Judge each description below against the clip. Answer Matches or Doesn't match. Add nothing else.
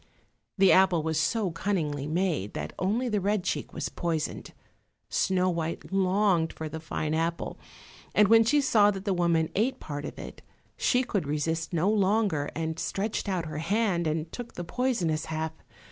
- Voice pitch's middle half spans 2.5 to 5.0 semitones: Matches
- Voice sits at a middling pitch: Matches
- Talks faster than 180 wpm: Doesn't match